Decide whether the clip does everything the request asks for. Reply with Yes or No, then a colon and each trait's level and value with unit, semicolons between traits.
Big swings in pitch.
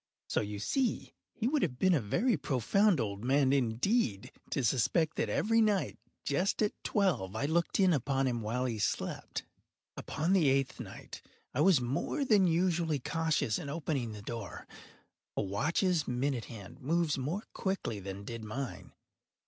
Yes: wide, 7.4 semitones